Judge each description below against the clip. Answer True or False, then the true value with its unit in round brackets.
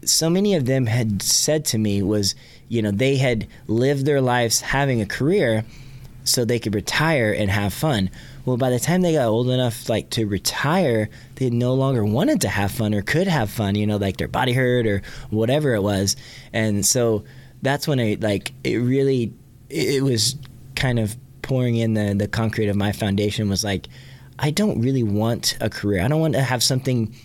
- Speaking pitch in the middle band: False (120 Hz)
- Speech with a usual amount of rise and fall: True (3.9 semitones)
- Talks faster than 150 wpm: True (205 wpm)